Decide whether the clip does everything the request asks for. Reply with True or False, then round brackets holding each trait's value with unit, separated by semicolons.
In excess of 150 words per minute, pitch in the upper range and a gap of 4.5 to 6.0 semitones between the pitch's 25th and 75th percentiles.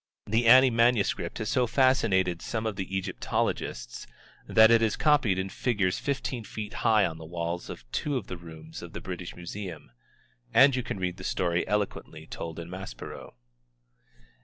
False (170 wpm; 100 Hz; 4.9 semitones)